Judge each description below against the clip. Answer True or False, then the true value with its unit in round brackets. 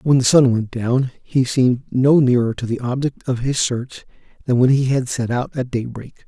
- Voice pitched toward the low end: True (125 Hz)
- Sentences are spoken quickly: True (220 wpm)